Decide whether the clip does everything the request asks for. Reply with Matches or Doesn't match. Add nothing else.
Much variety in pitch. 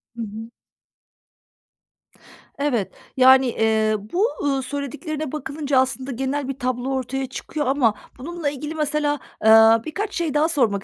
Doesn't match